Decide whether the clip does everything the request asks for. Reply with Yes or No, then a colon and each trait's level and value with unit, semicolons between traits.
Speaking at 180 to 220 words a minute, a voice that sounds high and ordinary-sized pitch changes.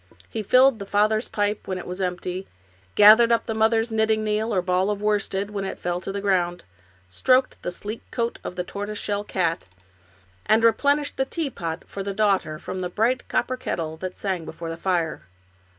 Yes: average, 200 wpm; high, 205 Hz; average, 3.4 semitones